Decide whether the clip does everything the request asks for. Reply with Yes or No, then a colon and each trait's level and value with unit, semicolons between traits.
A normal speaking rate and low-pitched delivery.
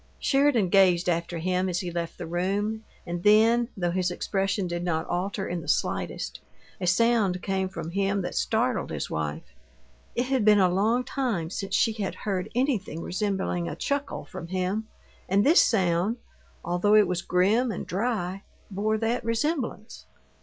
No: average, 165 wpm; high, 195 Hz